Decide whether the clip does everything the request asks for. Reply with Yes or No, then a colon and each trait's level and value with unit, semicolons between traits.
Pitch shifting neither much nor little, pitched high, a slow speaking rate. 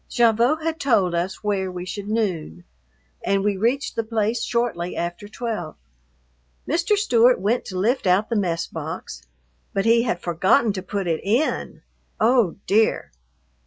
No: average, 4.4 semitones; high, 210 Hz; average, 155 wpm